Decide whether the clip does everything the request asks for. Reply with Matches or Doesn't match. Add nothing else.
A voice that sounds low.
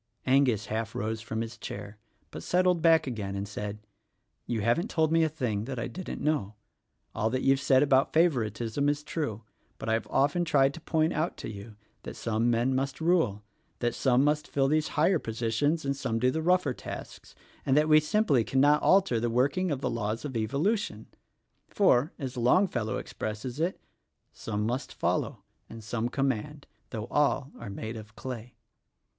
Matches